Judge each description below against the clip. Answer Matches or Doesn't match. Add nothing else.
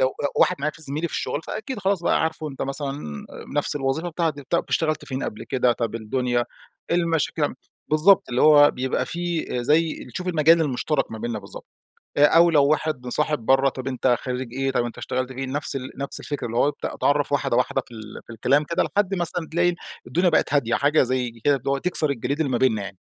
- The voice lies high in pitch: Doesn't match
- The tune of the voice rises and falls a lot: Doesn't match